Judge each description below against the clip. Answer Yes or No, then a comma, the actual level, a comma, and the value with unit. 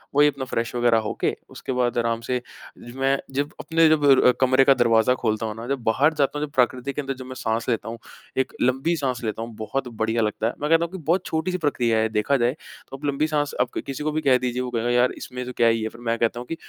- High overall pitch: No, low, 125 Hz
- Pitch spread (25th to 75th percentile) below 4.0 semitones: Yes, average, 3.4 semitones